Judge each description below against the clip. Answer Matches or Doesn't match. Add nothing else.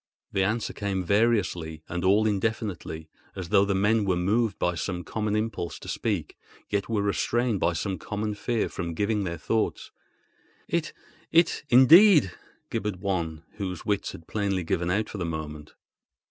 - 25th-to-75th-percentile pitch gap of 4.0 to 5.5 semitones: Doesn't match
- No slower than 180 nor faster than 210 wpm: Doesn't match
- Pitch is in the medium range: Doesn't match